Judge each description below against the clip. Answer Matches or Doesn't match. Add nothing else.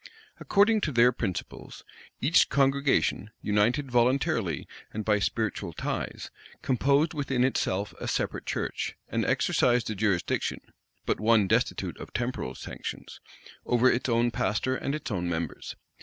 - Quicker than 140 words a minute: Doesn't match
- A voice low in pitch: Matches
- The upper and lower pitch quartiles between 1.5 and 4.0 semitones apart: Doesn't match